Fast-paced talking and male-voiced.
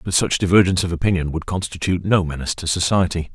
No: average, 195 wpm; male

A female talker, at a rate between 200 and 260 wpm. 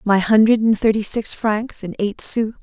Yes: female; fast, 205 wpm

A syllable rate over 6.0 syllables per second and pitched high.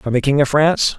No: 6.3 syllables/s; medium, 140 Hz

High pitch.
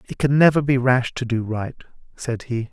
No: low, 125 Hz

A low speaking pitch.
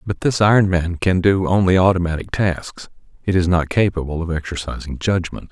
Yes: very low, 90 Hz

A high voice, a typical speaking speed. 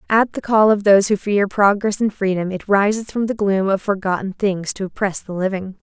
No: high, 200 Hz; fast, 225 wpm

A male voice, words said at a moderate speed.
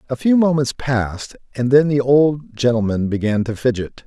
Yes: male; average, 175 wpm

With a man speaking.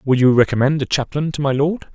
Yes: male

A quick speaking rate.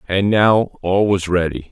No: average, 175 wpm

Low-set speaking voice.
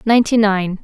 No: high, 210 Hz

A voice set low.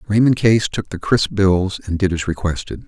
Yes: low, 100 Hz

